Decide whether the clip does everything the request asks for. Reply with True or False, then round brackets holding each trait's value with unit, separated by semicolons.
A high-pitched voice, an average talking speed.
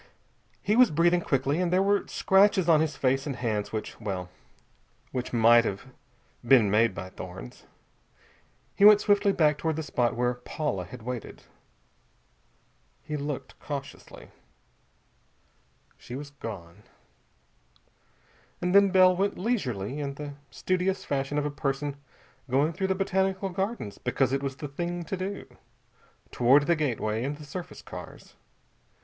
False (145 Hz; 145 wpm)